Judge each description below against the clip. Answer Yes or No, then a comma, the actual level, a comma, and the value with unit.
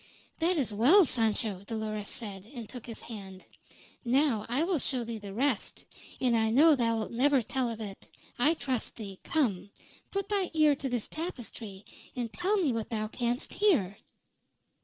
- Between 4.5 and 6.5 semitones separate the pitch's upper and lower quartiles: Yes, average, 5.0 semitones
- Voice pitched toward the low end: No, high, 235 Hz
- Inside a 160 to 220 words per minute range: Yes, average, 170 wpm